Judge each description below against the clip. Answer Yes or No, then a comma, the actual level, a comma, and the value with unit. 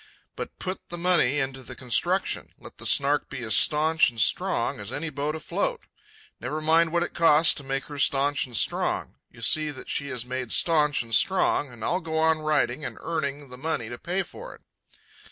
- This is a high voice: No, medium, 145 Hz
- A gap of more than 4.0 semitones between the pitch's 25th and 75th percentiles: No, average, 3.7 semitones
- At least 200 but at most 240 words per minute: Yes, fast, 205 wpm